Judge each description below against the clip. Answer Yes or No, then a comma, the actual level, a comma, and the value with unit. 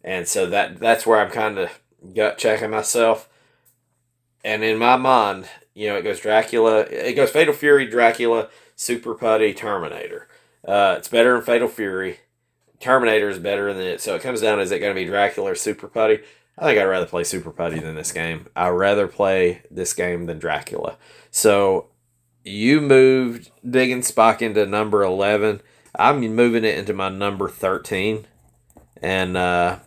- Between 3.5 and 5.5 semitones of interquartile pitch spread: Yes, average, 4.3 semitones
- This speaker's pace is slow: No, average, 175 wpm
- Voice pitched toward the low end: Yes, low, 115 Hz